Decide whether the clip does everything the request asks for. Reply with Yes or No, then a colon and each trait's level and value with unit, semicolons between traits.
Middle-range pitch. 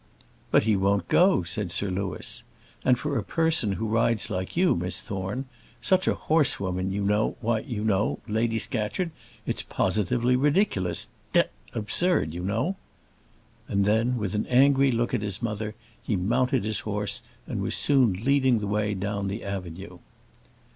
No: low, 105 Hz